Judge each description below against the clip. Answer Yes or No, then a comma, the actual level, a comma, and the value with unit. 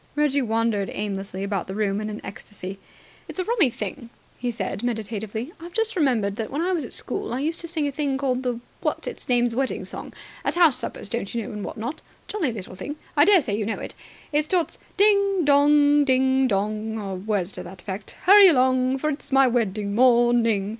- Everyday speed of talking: No, fast, 215 wpm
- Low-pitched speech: No, high, 245 Hz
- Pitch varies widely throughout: Yes, wide, 5.7 semitones